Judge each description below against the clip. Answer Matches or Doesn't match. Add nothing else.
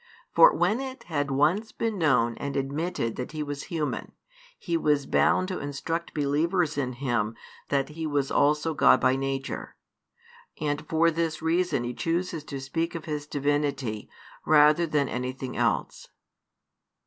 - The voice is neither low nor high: Matches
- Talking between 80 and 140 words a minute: Doesn't match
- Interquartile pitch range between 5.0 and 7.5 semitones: Doesn't match